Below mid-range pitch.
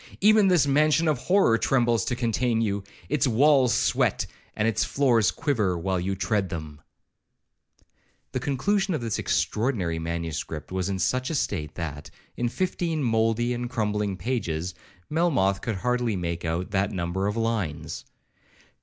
Yes: low, 110 Hz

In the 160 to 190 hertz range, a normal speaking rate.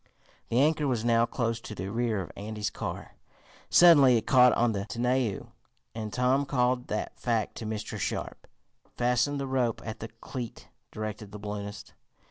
No: low, 115 Hz; average, 165 wpm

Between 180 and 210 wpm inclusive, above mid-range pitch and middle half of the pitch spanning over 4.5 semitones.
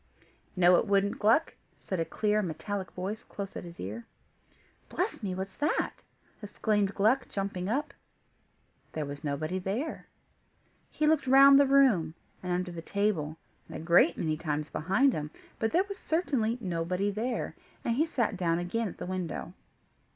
No: average, 165 wpm; high, 195 Hz; average, 5.3 semitones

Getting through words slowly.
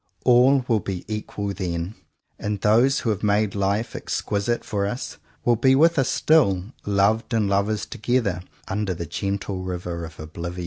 No: average, 170 wpm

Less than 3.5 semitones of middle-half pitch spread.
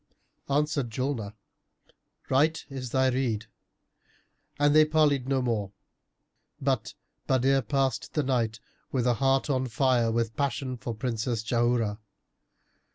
Yes: average, 3.0 semitones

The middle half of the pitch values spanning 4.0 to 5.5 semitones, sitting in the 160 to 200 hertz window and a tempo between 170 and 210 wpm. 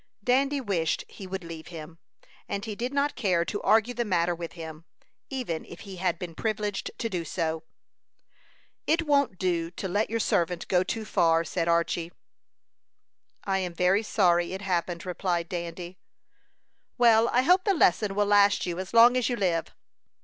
Yes: average, 4.6 semitones; high, 190 Hz; average, 175 wpm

